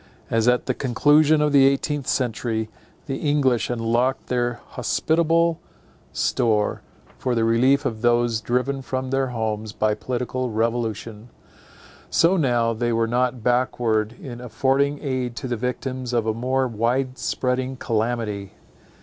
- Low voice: Yes, low, 125 Hz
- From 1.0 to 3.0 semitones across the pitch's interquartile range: Yes, narrow, 2.5 semitones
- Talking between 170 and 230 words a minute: No, average, 140 wpm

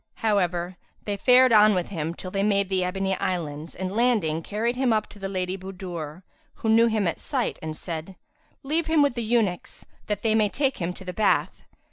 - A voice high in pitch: Yes, high, 195 Hz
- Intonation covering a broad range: No, average, 3.6 semitones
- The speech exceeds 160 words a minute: Yes, fast, 205 wpm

